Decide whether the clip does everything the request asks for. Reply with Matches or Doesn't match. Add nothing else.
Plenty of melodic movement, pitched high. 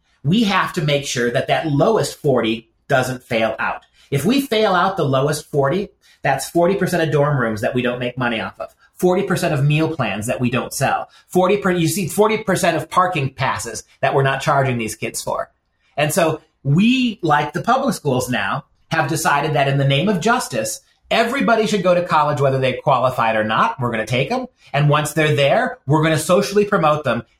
Doesn't match